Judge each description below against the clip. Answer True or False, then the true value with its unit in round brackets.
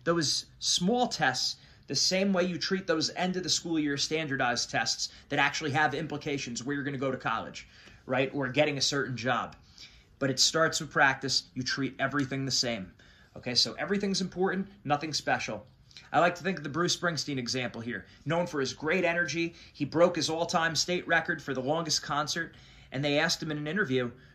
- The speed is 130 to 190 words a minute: False (200 wpm)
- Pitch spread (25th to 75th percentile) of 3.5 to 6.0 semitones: True (4.1 semitones)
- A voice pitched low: False (150 Hz)